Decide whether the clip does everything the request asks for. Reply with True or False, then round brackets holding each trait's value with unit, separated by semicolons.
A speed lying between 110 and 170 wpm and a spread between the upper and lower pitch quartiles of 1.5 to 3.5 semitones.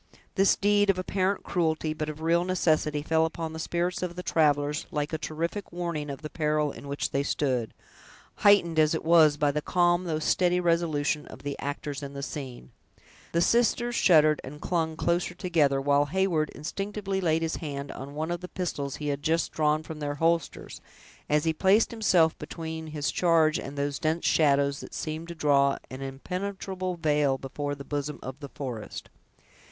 False (190 wpm; 3.1 semitones)